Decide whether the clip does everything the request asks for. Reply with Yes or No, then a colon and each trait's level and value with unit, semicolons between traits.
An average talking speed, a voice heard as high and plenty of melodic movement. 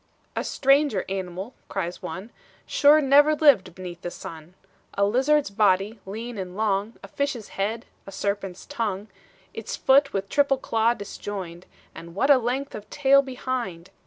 Yes: average, 155 wpm; high, 215 Hz; wide, 5.8 semitones